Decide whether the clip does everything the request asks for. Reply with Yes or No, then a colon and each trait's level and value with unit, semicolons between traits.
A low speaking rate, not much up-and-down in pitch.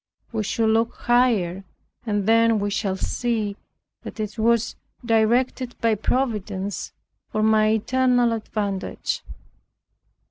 Yes: slow, 110 wpm; narrow, 2.2 semitones